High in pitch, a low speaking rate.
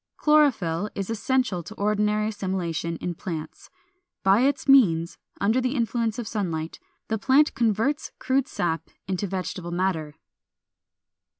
Yes: high, 205 Hz; slow, 125 wpm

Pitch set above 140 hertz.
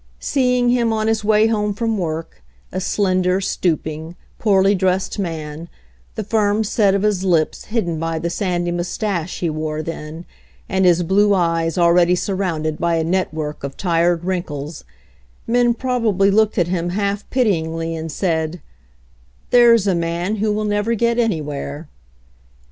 Yes: medium, 185 Hz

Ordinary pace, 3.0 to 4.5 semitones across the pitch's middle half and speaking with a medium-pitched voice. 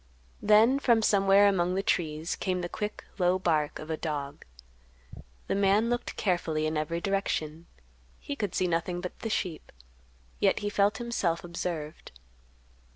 Yes: average, 155 wpm; average, 3.8 semitones; medium, 180 Hz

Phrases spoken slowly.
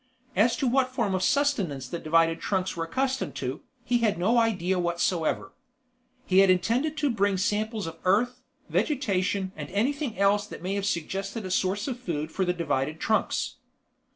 No: average, 175 wpm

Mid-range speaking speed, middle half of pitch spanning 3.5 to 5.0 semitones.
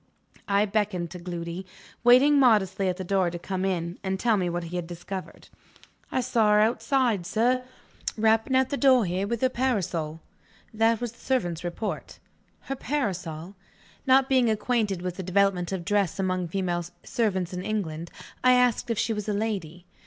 Yes: average, 175 wpm; average, 4.7 semitones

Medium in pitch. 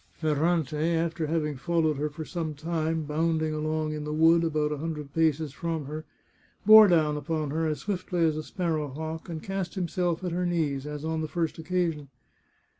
Yes: medium, 160 Hz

